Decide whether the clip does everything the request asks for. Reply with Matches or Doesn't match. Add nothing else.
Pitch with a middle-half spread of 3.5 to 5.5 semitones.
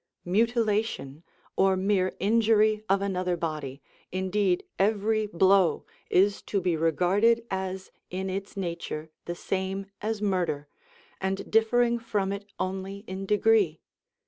Doesn't match